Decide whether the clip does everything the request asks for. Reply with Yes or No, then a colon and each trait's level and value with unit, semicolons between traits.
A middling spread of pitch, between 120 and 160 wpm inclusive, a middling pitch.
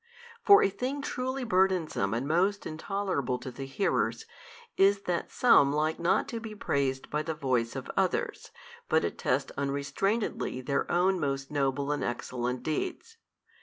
No: wide, 6.4 semitones; average, 155 wpm; medium, 155 Hz